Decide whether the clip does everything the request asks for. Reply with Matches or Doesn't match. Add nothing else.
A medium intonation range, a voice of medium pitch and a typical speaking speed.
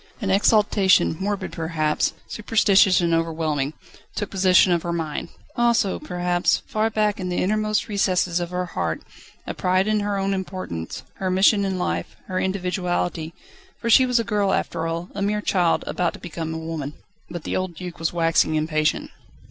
Matches